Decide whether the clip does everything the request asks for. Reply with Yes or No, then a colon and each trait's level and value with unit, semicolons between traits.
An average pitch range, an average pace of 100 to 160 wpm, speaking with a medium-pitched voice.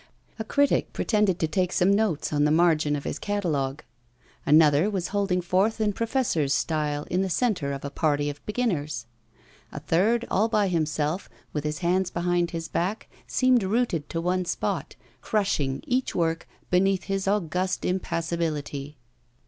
Yes: average, 4.9 semitones; average, 155 wpm; medium, 175 Hz